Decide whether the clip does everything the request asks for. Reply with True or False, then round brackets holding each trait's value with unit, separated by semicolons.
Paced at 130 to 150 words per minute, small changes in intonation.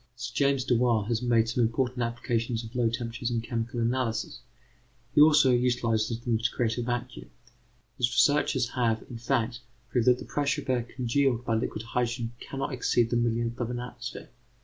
False (180 wpm; 1.5 semitones)